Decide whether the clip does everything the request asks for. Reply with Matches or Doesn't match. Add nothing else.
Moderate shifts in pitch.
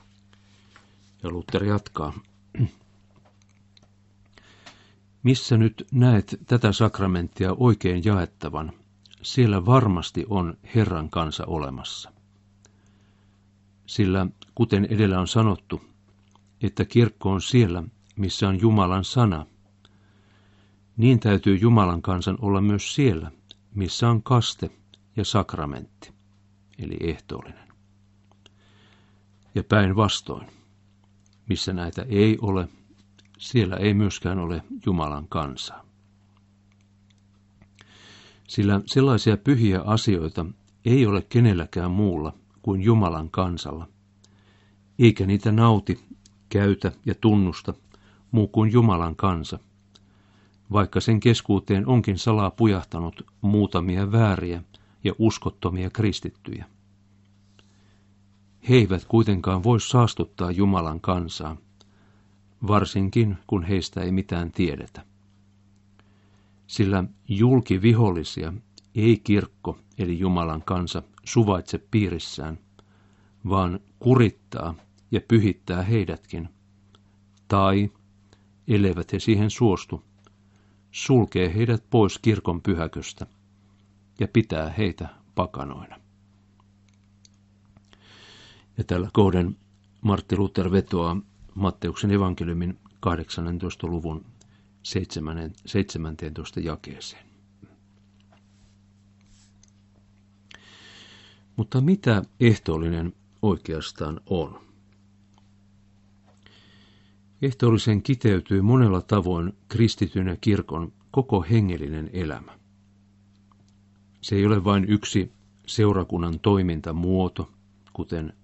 Doesn't match